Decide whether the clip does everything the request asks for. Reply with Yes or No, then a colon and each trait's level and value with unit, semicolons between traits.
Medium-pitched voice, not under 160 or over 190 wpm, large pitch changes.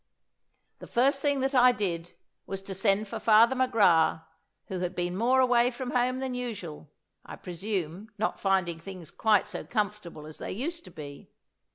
No: high, 210 Hz; average, 175 wpm; wide, 5.8 semitones